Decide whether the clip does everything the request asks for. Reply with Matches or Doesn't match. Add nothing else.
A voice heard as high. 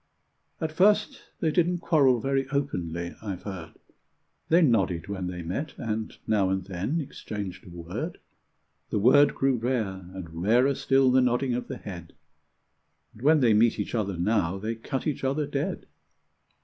Doesn't match